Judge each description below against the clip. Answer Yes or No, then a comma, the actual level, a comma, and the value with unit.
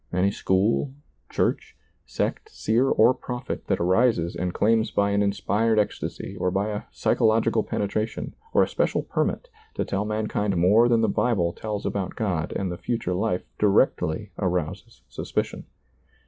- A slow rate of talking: No, average, 150 wpm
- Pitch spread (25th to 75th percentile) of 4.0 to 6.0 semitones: No, average, 3.4 semitones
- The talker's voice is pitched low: Yes, low, 105 Hz